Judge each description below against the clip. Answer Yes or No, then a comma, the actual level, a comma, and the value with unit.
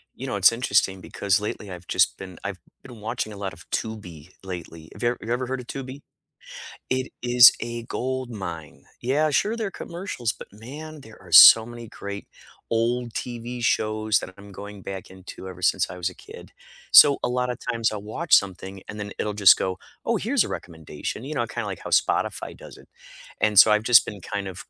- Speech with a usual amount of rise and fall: Yes, average, 4.3 semitones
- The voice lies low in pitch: Yes, low, 110 Hz